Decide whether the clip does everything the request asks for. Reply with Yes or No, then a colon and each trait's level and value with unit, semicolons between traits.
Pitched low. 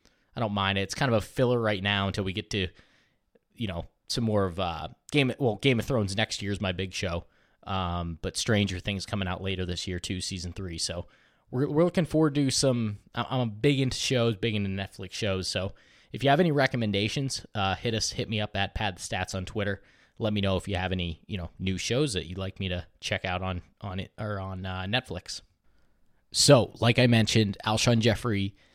Yes: low, 100 Hz